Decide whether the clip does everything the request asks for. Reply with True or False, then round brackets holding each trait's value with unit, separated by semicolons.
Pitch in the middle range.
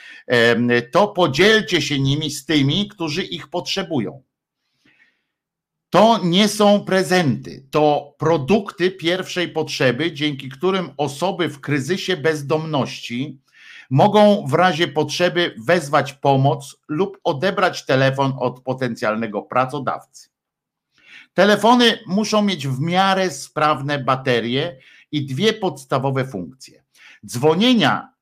True (160 Hz)